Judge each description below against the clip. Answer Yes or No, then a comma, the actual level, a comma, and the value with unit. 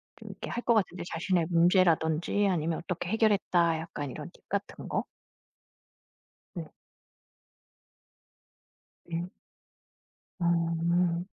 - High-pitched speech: No, medium, 170 Hz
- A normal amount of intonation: No, narrow, 1.8 semitones